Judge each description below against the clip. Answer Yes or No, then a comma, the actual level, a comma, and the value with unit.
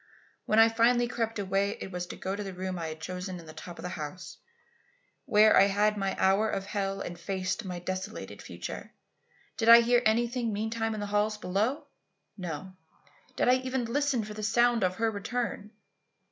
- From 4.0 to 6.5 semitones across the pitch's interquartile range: No, average, 3.4 semitones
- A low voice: No, high, 210 Hz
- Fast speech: No, average, 195 wpm